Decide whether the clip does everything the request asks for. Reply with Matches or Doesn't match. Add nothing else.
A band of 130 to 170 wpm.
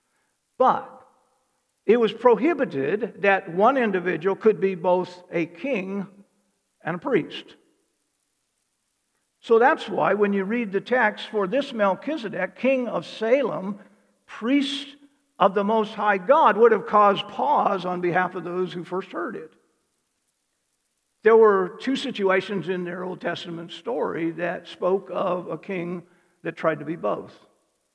Matches